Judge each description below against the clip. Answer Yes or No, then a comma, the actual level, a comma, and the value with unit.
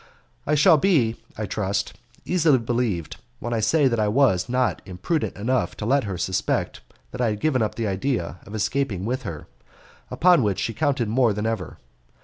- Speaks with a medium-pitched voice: No, low, 115 Hz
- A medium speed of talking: Yes, average, 185 wpm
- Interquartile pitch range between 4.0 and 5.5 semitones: Yes, average, 5.0 semitones